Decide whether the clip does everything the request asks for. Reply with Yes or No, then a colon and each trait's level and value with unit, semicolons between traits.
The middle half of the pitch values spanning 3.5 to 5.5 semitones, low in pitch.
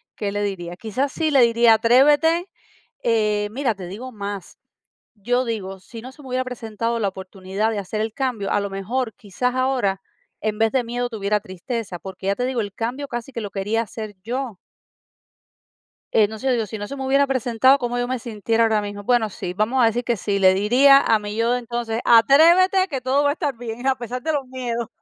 No: average, 3.8 semitones; high, 230 Hz